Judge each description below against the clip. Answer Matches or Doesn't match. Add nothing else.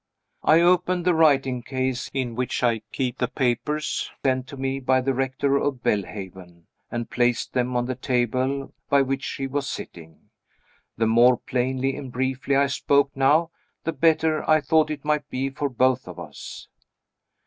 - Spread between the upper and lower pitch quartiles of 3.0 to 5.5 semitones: Doesn't match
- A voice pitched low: Matches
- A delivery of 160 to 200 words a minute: Matches